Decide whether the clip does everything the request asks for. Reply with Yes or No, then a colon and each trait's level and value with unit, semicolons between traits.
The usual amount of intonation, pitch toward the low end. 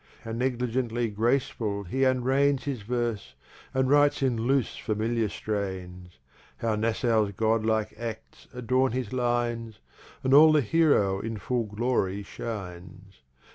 Yes: average, 3.6 semitones; low, 115 Hz